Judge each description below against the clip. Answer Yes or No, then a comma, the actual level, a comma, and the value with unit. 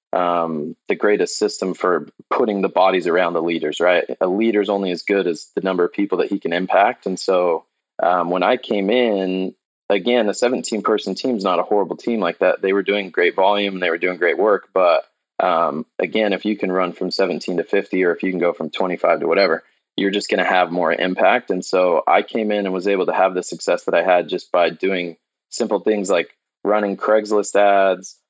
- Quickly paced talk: Yes, fast, 225 wpm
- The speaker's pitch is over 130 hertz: No, very low, 95 Hz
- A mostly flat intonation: Yes, narrow, 2.1 semitones